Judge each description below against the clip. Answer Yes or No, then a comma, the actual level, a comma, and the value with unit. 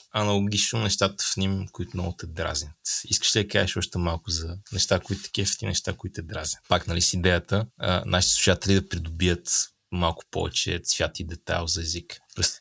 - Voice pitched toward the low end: Yes, very low, 95 Hz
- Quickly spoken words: Yes, fast, 185 wpm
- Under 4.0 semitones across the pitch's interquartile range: Yes, average, 2.8 semitones